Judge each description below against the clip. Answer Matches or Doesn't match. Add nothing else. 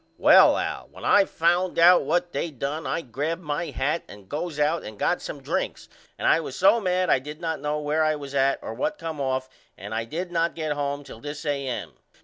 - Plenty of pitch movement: Doesn't match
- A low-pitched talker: Doesn't match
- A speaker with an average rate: Doesn't match